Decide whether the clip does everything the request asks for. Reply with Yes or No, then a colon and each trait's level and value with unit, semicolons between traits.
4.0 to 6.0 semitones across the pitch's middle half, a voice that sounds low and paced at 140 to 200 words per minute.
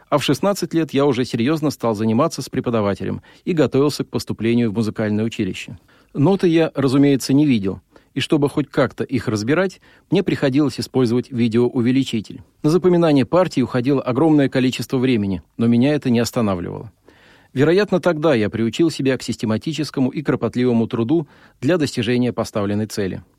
Yes: average, 4.3 semitones; low, 130 Hz; average, 150 wpm